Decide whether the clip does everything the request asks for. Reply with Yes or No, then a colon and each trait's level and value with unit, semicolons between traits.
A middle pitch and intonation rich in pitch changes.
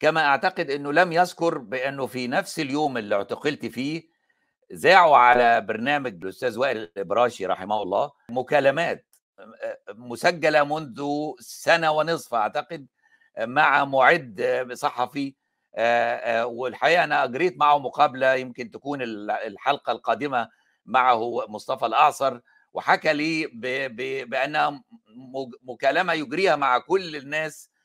No: medium, 145 Hz; average, 4.5 semitones